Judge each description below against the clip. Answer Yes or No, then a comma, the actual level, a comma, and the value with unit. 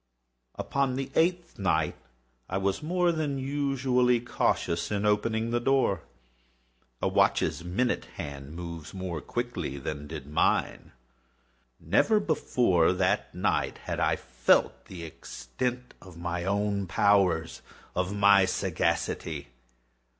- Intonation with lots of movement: Yes, wide, 7.0 semitones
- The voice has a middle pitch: No, low, 100 Hz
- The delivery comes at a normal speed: No, slow, 115 wpm